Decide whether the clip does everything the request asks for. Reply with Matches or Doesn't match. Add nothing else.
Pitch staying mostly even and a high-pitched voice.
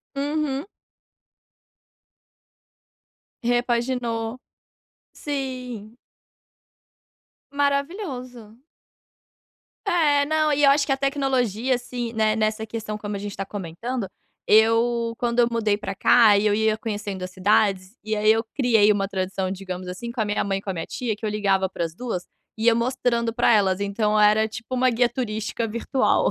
Doesn't match